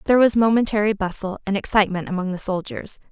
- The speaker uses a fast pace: No, average, 175 wpm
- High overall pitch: Yes, high, 200 Hz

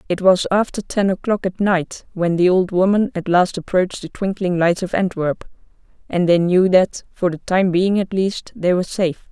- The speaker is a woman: Yes, female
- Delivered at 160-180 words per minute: No, fast, 205 wpm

